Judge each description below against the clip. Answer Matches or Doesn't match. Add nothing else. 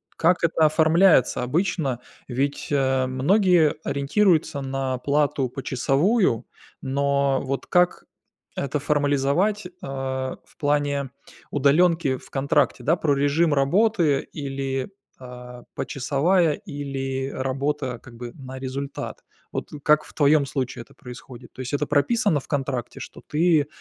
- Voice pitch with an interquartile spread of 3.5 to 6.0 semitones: Doesn't match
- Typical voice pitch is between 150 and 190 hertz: Doesn't match